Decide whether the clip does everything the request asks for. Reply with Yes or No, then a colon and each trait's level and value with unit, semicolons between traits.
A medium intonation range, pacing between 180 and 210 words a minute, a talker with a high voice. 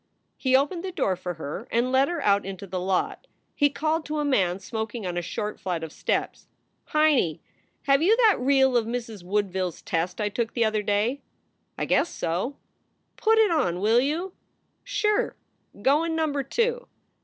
No: wide, 7.9 semitones; average, 190 wpm; high, 245 Hz